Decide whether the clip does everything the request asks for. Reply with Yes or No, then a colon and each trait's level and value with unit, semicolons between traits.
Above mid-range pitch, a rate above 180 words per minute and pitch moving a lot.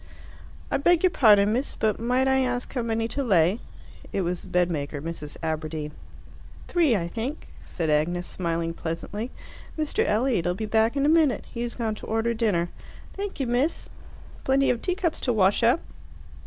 No: high, 225 Hz; average, 175 wpm; wide, 7.1 semitones